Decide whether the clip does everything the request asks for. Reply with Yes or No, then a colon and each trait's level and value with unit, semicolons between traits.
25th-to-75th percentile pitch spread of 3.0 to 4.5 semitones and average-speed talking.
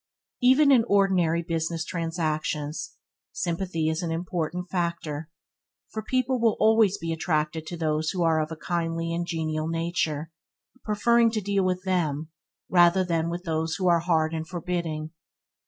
No: narrow, 2.6 semitones; average, 155 wpm